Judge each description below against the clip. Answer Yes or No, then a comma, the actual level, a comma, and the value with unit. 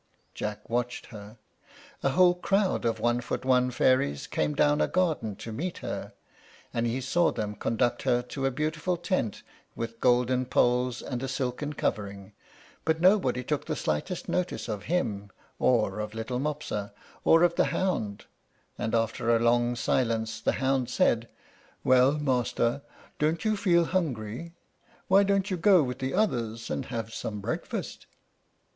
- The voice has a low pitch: Yes, low, 125 Hz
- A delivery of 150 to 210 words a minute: Yes, average, 160 wpm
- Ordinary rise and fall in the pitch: No, wide, 5.8 semitones